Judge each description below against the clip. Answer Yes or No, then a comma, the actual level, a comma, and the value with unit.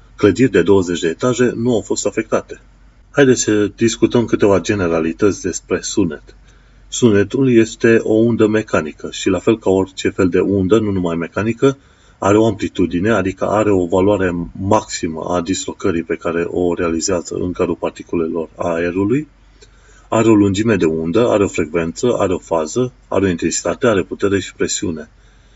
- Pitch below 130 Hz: Yes, low, 105 Hz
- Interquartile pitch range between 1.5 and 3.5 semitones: No, average, 4.2 semitones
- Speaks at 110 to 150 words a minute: No, average, 160 wpm